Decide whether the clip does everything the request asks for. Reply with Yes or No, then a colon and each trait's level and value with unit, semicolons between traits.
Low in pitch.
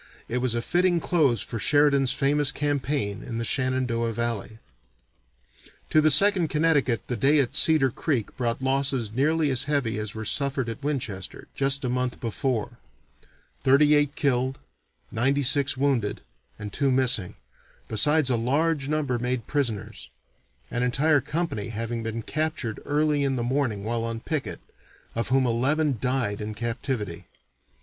Yes: low, 130 Hz